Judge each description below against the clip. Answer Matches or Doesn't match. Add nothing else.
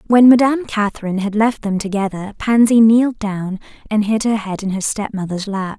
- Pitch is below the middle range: Doesn't match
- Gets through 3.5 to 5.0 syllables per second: Doesn't match